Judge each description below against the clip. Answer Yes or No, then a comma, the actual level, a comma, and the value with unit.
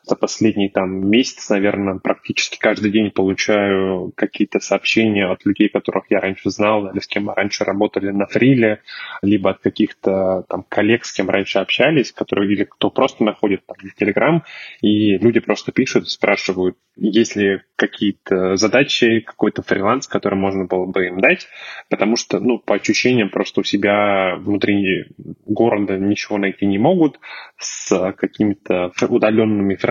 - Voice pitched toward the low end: Yes, low, 100 Hz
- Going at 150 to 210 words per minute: Yes, average, 155 wpm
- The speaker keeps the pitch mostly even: Yes, narrow, 2.0 semitones